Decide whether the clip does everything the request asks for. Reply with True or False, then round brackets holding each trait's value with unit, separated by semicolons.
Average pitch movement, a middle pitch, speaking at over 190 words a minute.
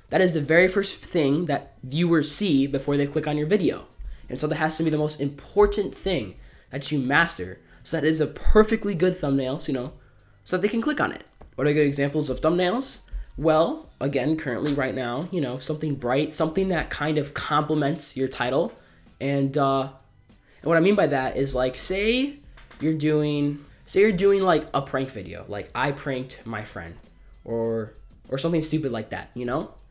True (3.7 semitones; 145 Hz; 200 wpm)